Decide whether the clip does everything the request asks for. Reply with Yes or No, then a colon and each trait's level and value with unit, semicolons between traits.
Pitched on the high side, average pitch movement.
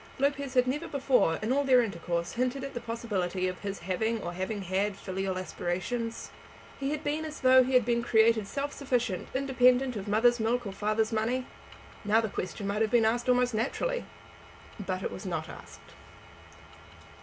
Yes: high, 230 Hz; average, 4.5 semitones